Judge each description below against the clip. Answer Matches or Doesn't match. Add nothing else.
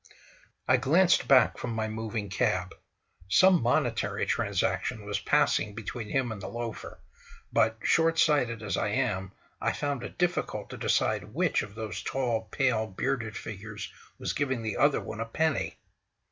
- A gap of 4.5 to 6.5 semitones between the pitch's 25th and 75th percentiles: Doesn't match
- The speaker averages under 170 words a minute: Matches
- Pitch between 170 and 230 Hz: Doesn't match